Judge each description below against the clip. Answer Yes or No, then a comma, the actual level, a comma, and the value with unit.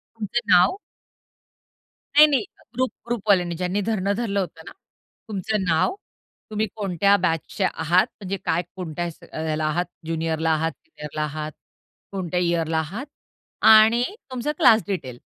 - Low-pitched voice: No, medium, 185 Hz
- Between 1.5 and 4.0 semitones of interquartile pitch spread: No, average, 5.0 semitones